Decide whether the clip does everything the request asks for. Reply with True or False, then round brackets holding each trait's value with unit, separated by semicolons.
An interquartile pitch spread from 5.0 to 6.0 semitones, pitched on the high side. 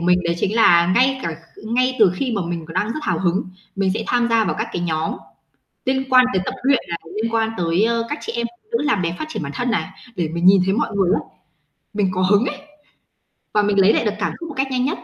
True (5.6 semitones; 210 Hz)